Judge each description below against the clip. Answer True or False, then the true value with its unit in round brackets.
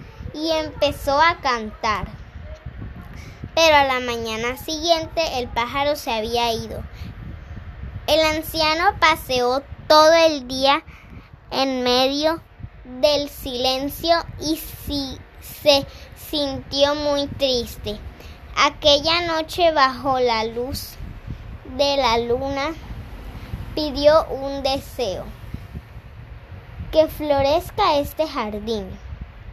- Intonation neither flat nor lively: True (4.0 semitones)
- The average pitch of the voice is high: True (280 Hz)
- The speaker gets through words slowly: True (90 wpm)